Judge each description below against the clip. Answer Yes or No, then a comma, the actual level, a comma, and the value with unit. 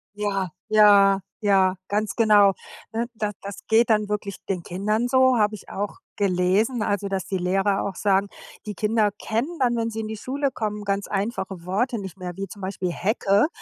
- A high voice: Yes, high, 205 Hz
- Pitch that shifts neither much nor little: No, narrow, 2.1 semitones